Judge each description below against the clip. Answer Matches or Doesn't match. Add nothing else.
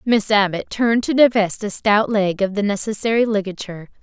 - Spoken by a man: Doesn't match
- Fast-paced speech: Doesn't match